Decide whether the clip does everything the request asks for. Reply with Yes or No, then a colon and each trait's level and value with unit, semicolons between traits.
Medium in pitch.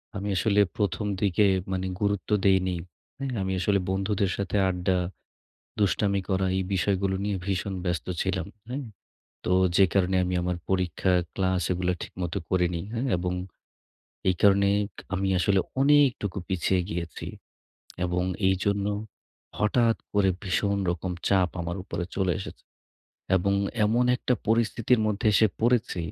No: very low, 95 Hz